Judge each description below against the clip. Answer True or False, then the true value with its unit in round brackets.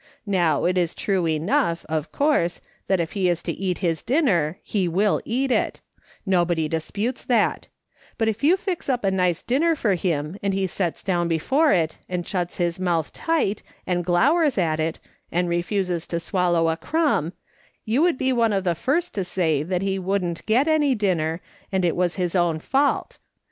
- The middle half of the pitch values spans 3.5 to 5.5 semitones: True (4.6 semitones)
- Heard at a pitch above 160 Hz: True (185 Hz)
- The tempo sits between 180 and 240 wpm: True (190 wpm)